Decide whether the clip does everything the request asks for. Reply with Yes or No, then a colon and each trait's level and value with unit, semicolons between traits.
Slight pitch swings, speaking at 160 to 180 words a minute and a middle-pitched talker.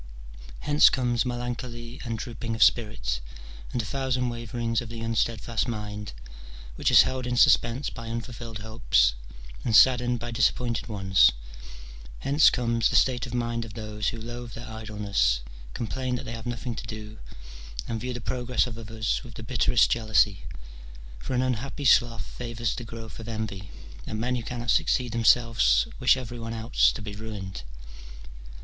No: narrow, 1.9 semitones; average, 170 wpm; low, 115 Hz